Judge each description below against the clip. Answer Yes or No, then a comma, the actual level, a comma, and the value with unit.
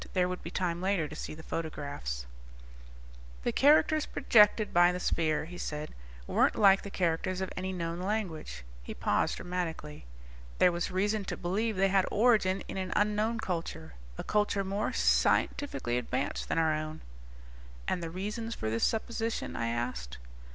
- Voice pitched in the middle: Yes, medium, 180 Hz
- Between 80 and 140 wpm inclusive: No, average, 165 wpm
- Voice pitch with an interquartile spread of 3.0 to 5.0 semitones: Yes, average, 4.7 semitones